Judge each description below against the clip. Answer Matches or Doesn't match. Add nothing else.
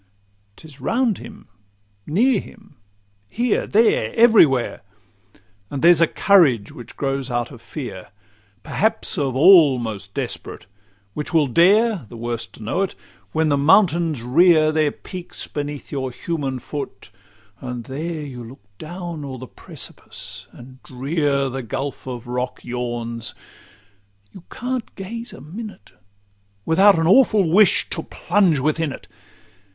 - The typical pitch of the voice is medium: Matches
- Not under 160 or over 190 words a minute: Doesn't match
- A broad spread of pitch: Matches